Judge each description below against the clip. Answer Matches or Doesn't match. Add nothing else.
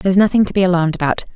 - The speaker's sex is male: Doesn't match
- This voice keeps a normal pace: Doesn't match